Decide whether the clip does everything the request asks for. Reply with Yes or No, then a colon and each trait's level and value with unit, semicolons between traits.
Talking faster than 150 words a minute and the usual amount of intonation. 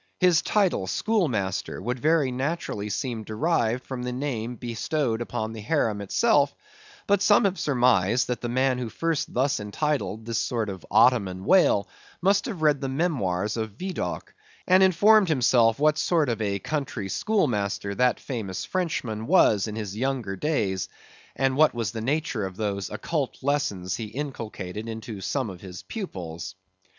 No: average, 160 wpm; wide, 6.3 semitones